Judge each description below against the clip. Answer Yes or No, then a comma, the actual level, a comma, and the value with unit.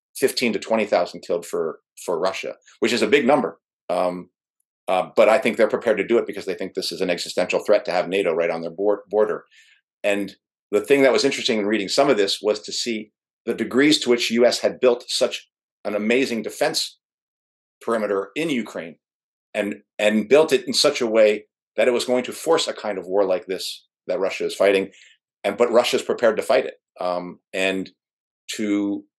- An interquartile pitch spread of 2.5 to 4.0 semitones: No, average, 4.8 semitones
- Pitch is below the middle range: Yes, low, 110 Hz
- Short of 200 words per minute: No, fast, 205 wpm